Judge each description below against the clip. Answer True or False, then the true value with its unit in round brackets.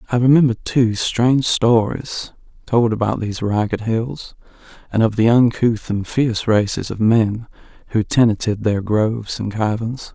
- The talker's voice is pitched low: True (115 Hz)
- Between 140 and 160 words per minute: True (150 wpm)